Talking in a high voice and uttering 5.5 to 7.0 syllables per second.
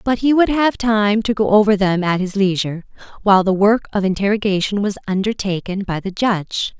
Yes: high, 205 Hz; 5.6 syllables/s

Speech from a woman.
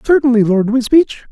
No: male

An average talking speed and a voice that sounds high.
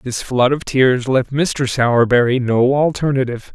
No: average, 150 wpm; low, 130 Hz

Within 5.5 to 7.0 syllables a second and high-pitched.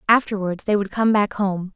No: 5.0 syllables/s; high, 200 Hz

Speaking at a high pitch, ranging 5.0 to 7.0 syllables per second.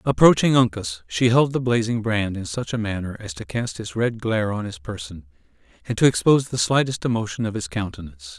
No: low, 105 Hz; 5.7 syllables/s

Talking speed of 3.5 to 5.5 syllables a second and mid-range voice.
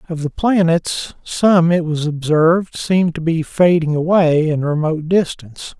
Yes: 4.5 syllables/s; medium, 165 Hz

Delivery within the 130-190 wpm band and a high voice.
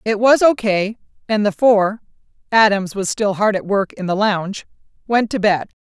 Yes: average, 175 wpm; high, 205 Hz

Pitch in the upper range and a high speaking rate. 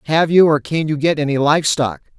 No: medium, 150 Hz; fast, 245 wpm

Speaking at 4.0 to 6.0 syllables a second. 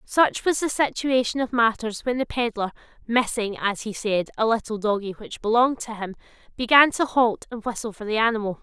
Yes: 5.4 syllables/s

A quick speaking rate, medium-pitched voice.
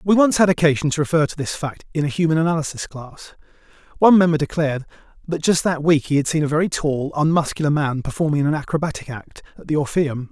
Yes: fast, 215 wpm; medium, 155 Hz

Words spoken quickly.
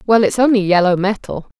No: average, 190 wpm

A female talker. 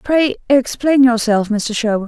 Yes: female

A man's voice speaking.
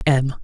Yes: male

